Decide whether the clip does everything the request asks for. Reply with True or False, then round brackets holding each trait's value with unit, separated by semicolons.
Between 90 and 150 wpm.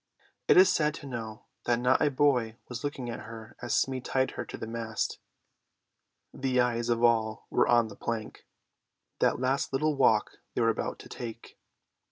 False (185 wpm)